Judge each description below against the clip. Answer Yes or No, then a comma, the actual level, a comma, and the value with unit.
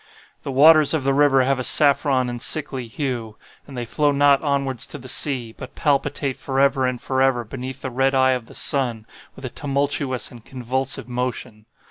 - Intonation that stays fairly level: Yes, narrow, 1.9 semitones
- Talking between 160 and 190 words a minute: Yes, average, 185 wpm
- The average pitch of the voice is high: No, low, 130 Hz